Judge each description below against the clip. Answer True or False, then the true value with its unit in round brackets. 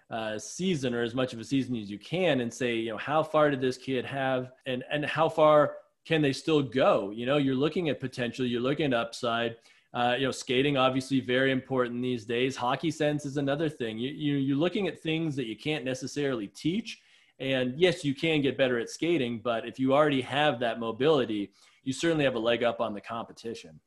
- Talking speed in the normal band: False (220 wpm)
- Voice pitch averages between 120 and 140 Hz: True (130 Hz)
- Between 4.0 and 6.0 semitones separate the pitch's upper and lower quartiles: False (3.6 semitones)